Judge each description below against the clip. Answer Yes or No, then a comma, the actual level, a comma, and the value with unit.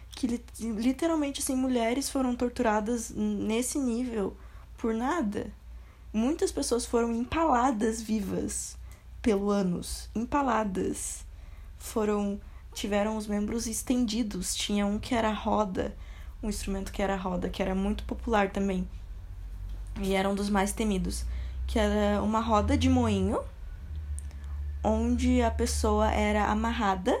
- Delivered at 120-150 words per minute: Yes, average, 125 wpm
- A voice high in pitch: Yes, high, 210 Hz